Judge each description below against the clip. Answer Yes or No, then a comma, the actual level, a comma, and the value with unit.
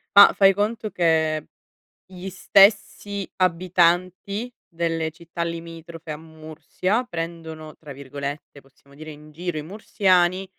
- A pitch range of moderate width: Yes, average, 3.0 semitones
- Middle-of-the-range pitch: Yes, medium, 170 Hz